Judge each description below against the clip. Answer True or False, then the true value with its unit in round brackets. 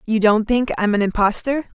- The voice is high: True (220 Hz)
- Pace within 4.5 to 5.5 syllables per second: True (5.1 syllables/s)